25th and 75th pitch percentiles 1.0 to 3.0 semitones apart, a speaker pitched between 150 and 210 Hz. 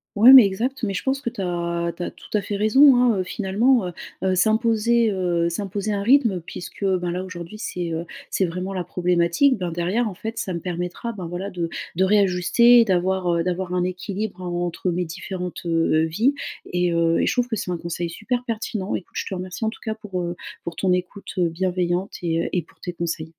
No: average, 3.6 semitones; medium, 185 Hz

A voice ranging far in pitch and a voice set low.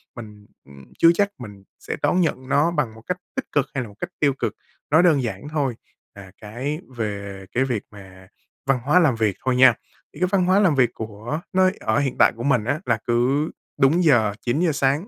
Yes: wide, 5.9 semitones; low, 130 Hz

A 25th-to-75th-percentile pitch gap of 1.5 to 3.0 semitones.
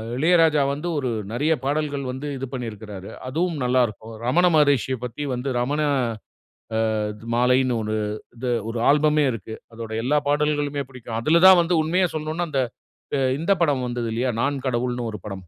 No: average, 3.8 semitones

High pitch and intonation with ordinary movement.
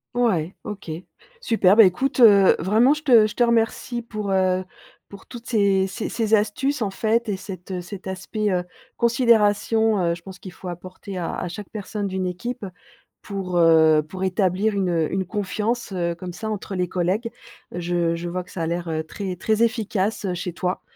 Yes: high, 195 Hz; average, 3.4 semitones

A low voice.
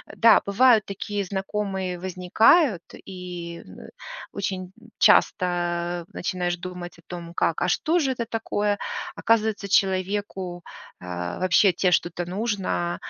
No: medium, 185 Hz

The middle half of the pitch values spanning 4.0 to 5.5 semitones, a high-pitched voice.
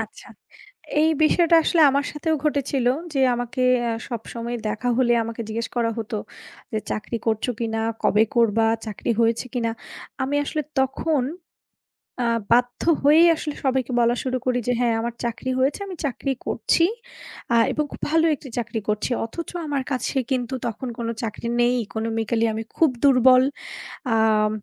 No: average, 3.2 semitones; high, 245 Hz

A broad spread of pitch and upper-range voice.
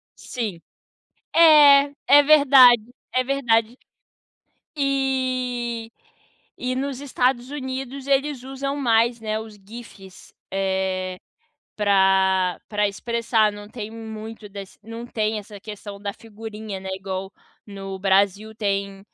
No: average, 4.4 semitones; high, 225 Hz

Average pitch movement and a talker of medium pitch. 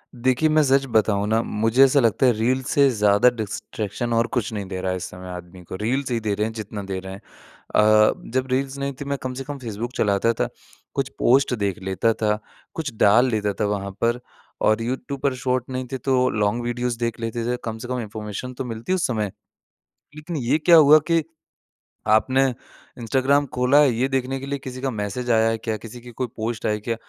No: average, 3.6 semitones; low, 120 Hz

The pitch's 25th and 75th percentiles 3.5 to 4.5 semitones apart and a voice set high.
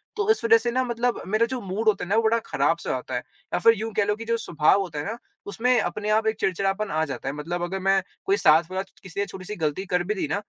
Yes: average, 4.1 semitones; high, 200 Hz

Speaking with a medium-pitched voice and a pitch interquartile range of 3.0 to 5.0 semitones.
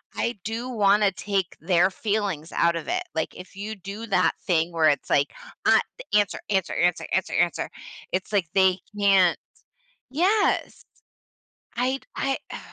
No: high, 195 Hz; average, 3.5 semitones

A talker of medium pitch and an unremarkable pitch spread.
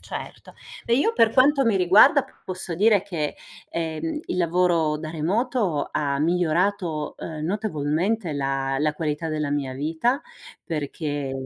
Yes: medium, 165 Hz; average, 5.0 semitones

